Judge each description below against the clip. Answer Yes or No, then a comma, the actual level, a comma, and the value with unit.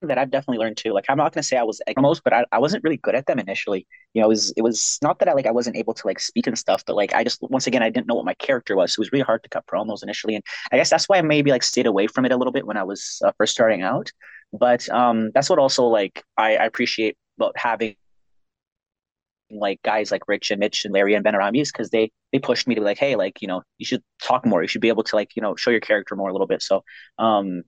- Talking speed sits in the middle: No, fast, 305 wpm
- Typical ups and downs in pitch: Yes, average, 3.8 semitones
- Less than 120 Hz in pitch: Yes, low, 110 Hz